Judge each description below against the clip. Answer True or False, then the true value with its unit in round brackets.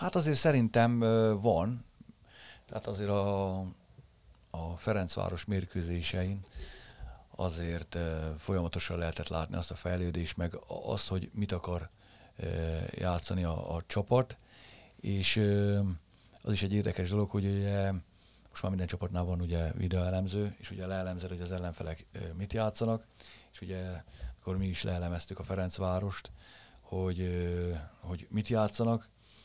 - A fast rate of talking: False (135 wpm)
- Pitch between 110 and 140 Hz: False (95 Hz)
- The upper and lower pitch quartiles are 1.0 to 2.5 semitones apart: False (2.9 semitones)